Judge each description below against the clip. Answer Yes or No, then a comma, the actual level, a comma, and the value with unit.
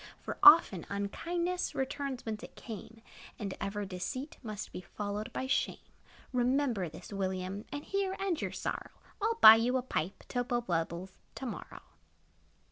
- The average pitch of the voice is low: No, high, 225 Hz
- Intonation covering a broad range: Yes, wide, 5.9 semitones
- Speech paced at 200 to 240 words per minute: No, average, 160 wpm